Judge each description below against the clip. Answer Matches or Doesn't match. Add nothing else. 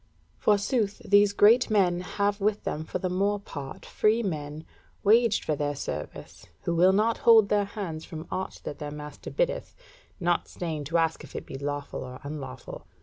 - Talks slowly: Doesn't match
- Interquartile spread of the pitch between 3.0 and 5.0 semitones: Doesn't match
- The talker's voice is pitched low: Doesn't match